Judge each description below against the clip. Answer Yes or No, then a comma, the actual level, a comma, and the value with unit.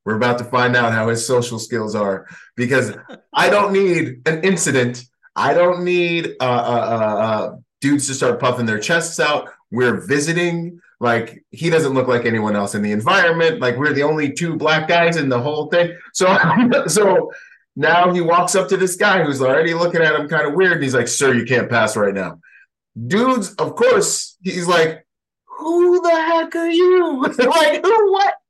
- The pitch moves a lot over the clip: Yes, wide, 7.5 semitones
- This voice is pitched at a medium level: Yes, medium, 160 Hz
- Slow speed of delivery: No, average, 190 wpm